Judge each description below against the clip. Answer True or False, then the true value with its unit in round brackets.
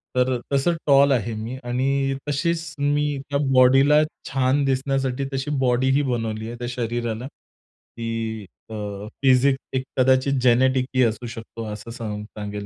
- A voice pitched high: False (130 Hz)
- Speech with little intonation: False (3.0 semitones)